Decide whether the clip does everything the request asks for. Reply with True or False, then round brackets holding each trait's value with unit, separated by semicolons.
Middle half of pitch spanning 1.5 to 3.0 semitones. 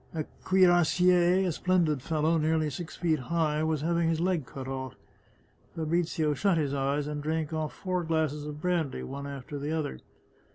True (2.6 semitones)